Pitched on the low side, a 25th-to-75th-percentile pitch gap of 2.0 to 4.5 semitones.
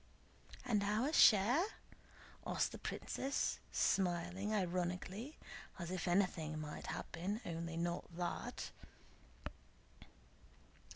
No: medium, 185 Hz; average, 3.6 semitones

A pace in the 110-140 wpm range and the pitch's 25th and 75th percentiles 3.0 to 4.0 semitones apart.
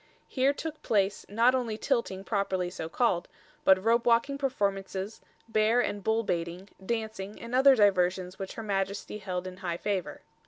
No: average, 160 wpm; average, 3.6 semitones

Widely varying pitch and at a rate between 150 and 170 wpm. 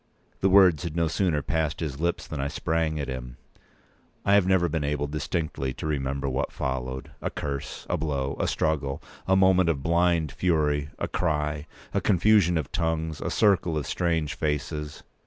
No: average, 3.2 semitones; average, 155 wpm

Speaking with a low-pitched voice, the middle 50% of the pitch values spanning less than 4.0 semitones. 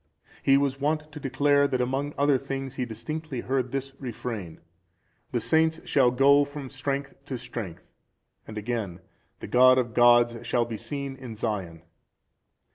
Yes: low, 130 Hz; average, 2.9 semitones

